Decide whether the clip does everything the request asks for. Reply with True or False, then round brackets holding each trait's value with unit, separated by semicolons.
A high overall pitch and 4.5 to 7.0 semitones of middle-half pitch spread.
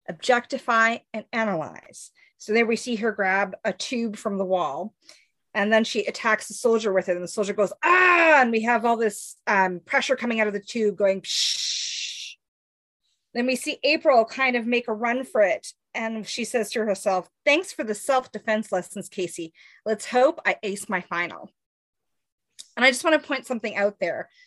False (225 Hz; 3.7 semitones)